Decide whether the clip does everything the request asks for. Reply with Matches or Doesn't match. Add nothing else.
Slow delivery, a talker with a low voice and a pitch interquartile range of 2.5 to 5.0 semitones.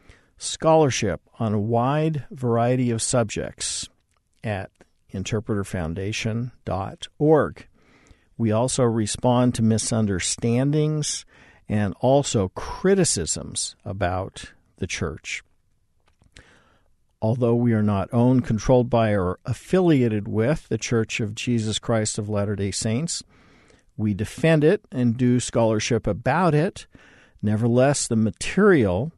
Matches